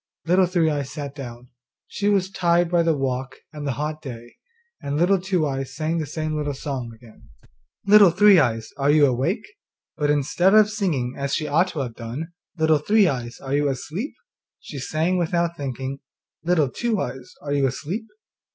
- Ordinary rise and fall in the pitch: Yes, average, 4.6 semitones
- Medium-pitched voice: Yes, medium, 150 Hz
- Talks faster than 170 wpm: Yes, average, 185 wpm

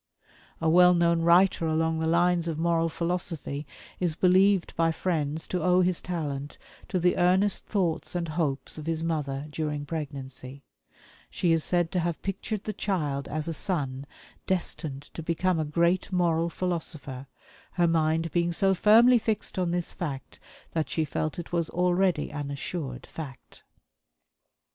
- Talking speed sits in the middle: Yes, average, 160 wpm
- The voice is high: No, medium, 165 Hz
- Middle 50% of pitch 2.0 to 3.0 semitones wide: Yes, average, 2.7 semitones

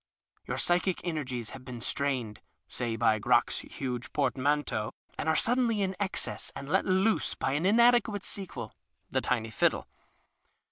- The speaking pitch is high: No, medium, 145 Hz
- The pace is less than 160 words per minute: Yes, average, 145 wpm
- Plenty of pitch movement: Yes, wide, 7.7 semitones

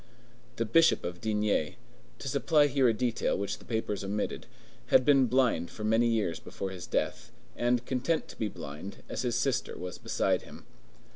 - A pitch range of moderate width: Yes, average, 4.4 semitones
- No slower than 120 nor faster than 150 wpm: No, average, 170 wpm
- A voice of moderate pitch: No, low, 115 Hz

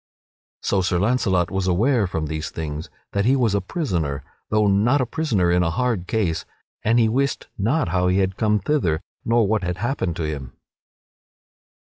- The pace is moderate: Yes, average, 180 wpm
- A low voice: Yes, low, 100 Hz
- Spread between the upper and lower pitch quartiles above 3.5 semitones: Yes, average, 5.0 semitones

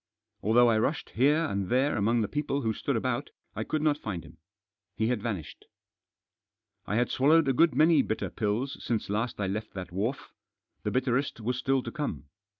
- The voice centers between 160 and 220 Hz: No, low, 120 Hz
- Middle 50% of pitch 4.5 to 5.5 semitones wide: Yes, average, 4.8 semitones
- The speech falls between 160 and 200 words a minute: Yes, average, 195 wpm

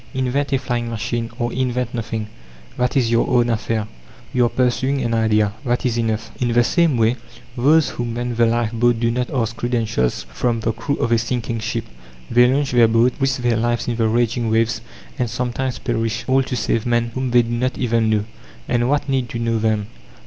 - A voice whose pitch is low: Yes, low, 120 Hz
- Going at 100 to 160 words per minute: No, fast, 205 wpm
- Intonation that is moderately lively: No, narrow, 1.6 semitones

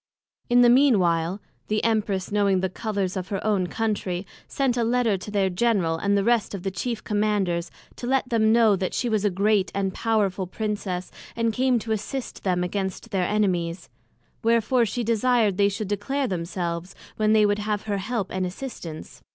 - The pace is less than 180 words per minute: No, average, 190 wpm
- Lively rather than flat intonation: No, average, 3.4 semitones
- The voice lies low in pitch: No, high, 205 Hz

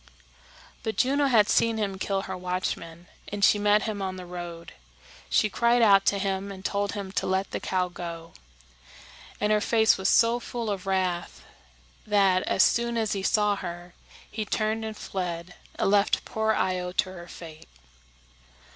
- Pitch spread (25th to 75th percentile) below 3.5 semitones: Yes, average, 2.9 semitones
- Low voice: No, high, 195 Hz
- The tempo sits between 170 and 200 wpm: Yes, average, 175 wpm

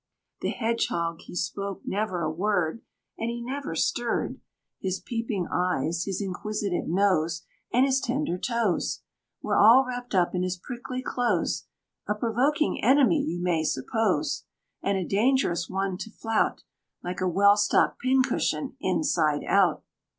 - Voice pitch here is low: No, high, 200 Hz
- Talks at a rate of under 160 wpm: Yes, average, 145 wpm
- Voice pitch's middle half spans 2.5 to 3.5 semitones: No, average, 5.0 semitones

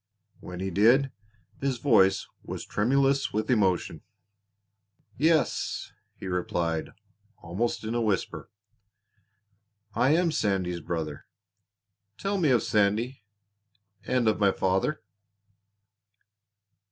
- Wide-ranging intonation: Yes, wide, 6.1 semitones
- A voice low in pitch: Yes, low, 110 Hz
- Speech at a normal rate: No, slow, 100 wpm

